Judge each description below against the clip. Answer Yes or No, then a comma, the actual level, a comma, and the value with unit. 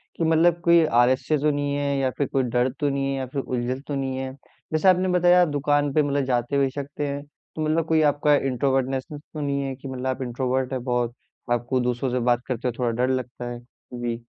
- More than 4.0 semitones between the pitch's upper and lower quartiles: No, narrow, 2.4 semitones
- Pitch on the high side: No, low, 135 Hz